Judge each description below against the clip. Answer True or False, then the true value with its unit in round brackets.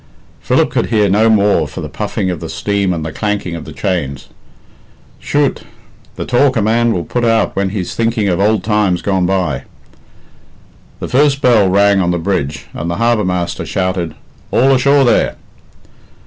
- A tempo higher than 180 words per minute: False (175 wpm)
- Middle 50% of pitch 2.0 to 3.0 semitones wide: False (4.2 semitones)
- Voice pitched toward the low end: True (100 Hz)